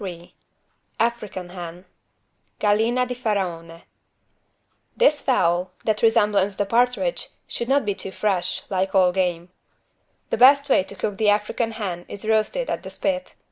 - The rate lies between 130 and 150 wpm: Yes, average, 145 wpm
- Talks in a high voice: Yes, high, 205 Hz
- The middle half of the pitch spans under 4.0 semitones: No, average, 4.4 semitones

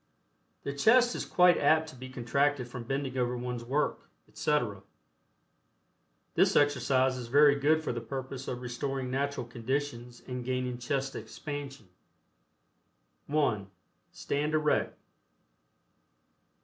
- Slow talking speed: Yes, slow, 120 wpm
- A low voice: Yes, low, 130 Hz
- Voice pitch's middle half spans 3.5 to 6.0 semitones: No, average, 2.8 semitones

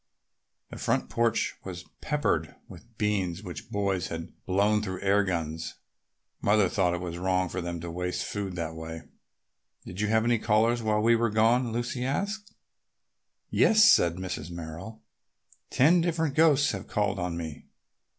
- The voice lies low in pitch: Yes, low, 100 Hz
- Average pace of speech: Yes, average, 160 wpm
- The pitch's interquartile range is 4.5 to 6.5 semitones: Yes, average, 5.0 semitones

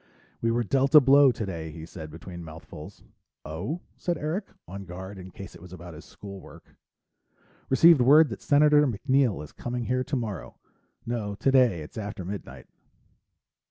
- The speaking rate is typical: Yes, average, 160 wpm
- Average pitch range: No, wide, 7.1 semitones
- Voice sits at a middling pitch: No, low, 110 Hz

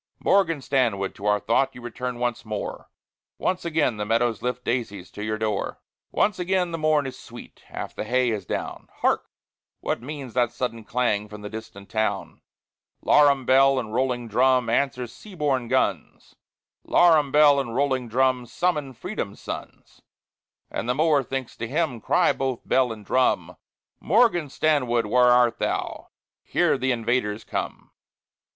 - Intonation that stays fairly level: No, average, 3.7 semitones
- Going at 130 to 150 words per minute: No, average, 160 wpm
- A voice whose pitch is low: Yes, low, 125 Hz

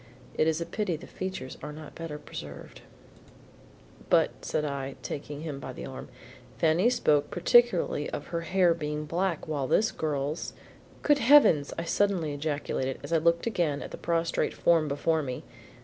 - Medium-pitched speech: Yes, medium, 160 Hz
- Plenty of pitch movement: No, average, 2.7 semitones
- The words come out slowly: No, average, 165 wpm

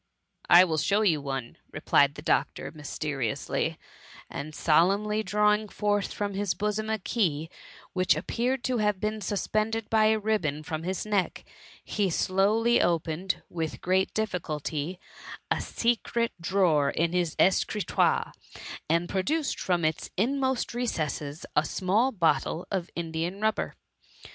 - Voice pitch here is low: No, high, 190 Hz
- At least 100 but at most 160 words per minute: Yes, slow, 135 wpm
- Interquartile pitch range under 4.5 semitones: No, average, 4.8 semitones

